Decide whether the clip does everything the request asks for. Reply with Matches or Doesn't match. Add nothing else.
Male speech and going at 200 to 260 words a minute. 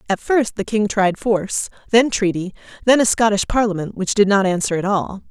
Doesn't match